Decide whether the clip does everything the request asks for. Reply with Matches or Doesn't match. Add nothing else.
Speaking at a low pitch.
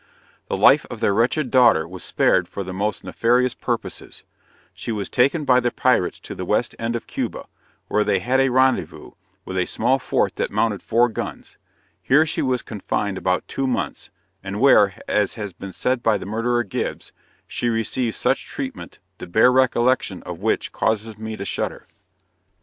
Matches